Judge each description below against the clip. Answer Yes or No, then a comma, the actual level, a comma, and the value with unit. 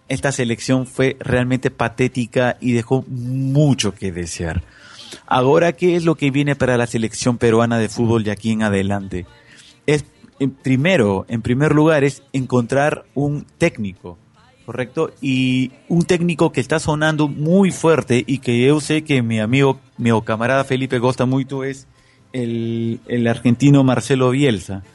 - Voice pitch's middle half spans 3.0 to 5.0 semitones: Yes, average, 3.3 semitones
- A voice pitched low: Yes, low, 130 Hz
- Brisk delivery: No, average, 150 wpm